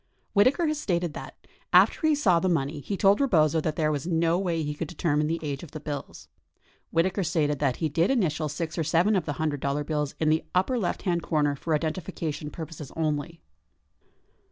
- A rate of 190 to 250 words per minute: Yes, average, 200 wpm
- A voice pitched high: No, medium, 160 Hz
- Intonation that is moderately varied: Yes, average, 3.0 semitones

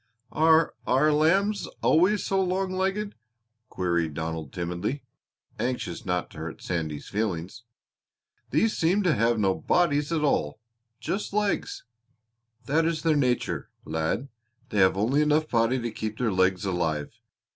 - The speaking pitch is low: Yes, low, 125 Hz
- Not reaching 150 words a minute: Yes, average, 140 wpm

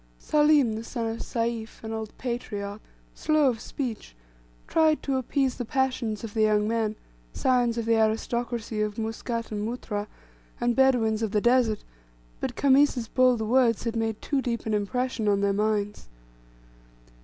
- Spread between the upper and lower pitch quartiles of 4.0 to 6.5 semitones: No, narrow, 2.6 semitones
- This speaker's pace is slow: No, average, 160 wpm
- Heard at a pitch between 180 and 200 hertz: No, high, 230 Hz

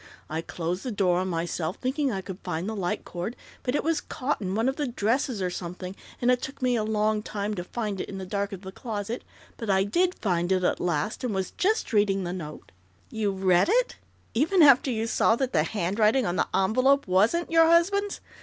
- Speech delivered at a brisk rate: Yes, fast, 230 wpm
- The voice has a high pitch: Yes, high, 210 Hz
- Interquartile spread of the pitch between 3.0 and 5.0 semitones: No, wide, 5.5 semitones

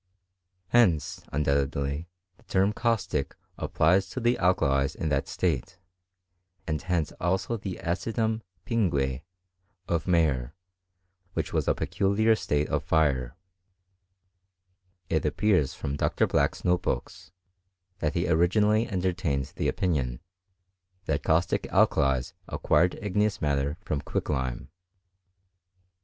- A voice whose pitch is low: Yes, very low, 85 Hz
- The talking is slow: Yes, slow, 115 wpm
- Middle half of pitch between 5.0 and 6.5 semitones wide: Yes, wide, 5.5 semitones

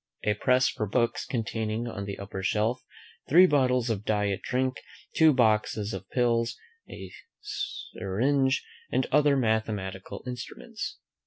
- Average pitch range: Yes, average, 3.8 semitones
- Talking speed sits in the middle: No, slow, 130 wpm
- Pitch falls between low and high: No, low, 115 Hz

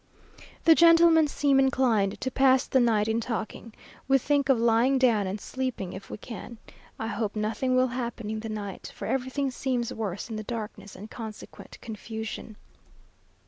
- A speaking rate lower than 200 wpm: Yes, average, 170 wpm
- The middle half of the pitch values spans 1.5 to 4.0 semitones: Yes, average, 3.4 semitones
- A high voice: Yes, high, 235 Hz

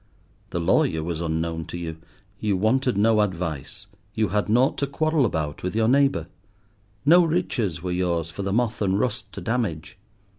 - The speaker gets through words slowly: No, average, 175 wpm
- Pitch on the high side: No, low, 100 Hz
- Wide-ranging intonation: Yes, wide, 6.4 semitones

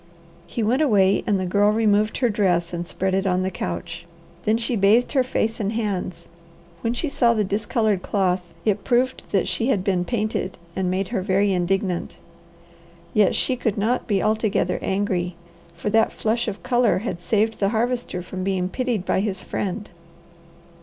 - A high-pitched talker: Yes, high, 205 Hz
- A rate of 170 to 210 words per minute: Yes, average, 180 wpm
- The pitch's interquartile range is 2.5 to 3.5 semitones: Yes, average, 3.2 semitones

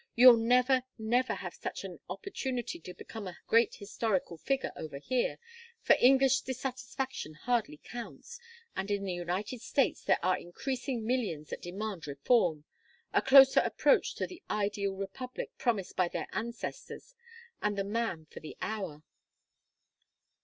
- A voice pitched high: Yes, high, 225 Hz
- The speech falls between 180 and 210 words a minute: No, average, 145 wpm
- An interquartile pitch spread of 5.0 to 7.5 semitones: Yes, wide, 5.4 semitones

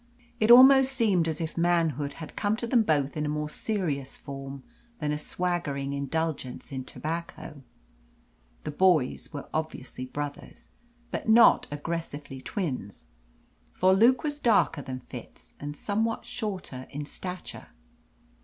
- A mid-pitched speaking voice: Yes, medium, 160 Hz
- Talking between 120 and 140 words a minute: Yes, slow, 135 wpm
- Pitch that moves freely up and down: Yes, wide, 6.1 semitones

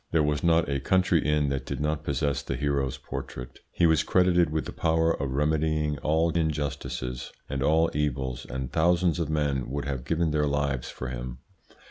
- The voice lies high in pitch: No, very low, 75 Hz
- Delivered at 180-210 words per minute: Yes, average, 185 wpm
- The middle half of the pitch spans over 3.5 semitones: No, average, 2.9 semitones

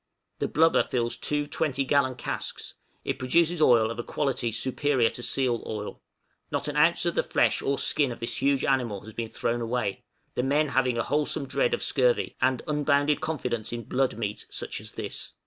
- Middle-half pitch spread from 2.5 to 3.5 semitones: No, average, 3.9 semitones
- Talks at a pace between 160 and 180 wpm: No, average, 195 wpm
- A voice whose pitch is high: No, low, 130 Hz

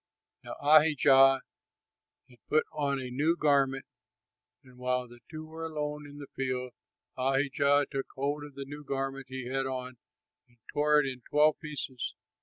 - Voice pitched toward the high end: No, low, 135 Hz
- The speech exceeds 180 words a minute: No, average, 160 wpm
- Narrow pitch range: Yes, narrow, 2.1 semitones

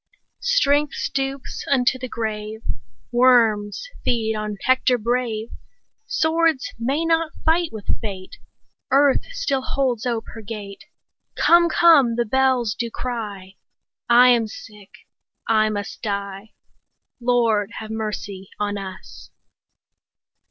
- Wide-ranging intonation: No, average, 4.0 semitones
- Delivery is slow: Yes, slow, 115 wpm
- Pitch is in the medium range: No, high, 235 Hz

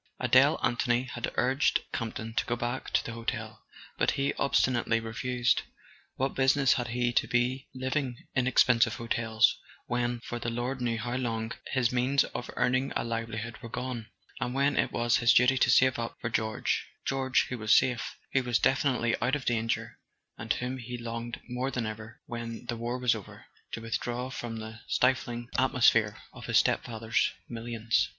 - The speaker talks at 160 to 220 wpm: Yes, average, 175 wpm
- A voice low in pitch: Yes, low, 120 Hz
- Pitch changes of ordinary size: No, narrow, 1.8 semitones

